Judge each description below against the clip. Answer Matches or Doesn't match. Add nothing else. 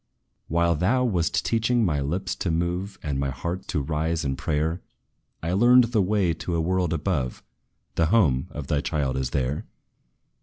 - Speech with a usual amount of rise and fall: Matches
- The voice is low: Matches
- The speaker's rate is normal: Matches